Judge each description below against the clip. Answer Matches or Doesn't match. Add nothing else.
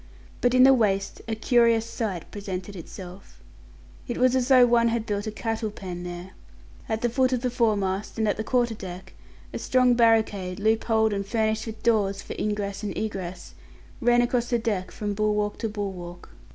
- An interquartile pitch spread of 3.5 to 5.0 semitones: Doesn't match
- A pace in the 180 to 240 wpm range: Matches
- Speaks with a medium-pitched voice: Doesn't match